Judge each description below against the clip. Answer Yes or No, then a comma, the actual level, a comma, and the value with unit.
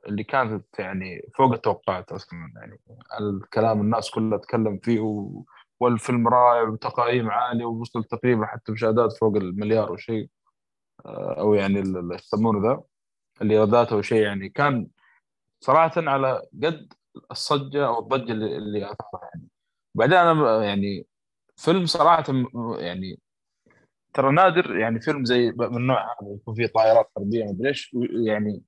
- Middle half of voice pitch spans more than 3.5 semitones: No, average, 2.8 semitones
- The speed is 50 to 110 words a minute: No, average, 130 wpm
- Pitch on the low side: Yes, low, 115 Hz